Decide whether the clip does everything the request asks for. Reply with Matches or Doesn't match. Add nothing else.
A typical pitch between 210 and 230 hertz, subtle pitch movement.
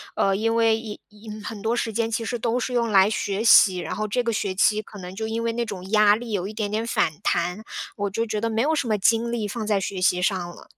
Matches